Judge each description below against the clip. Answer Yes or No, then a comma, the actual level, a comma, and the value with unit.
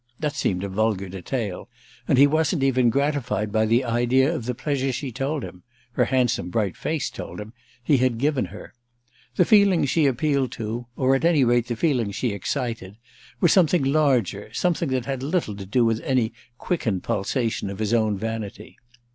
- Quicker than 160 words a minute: Yes, average, 180 wpm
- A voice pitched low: Yes, low, 125 Hz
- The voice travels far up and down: No, average, 4.3 semitones